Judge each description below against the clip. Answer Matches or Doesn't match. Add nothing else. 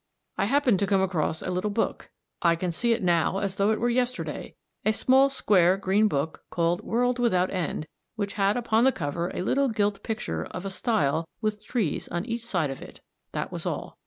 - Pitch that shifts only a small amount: Doesn't match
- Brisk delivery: Matches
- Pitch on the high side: Matches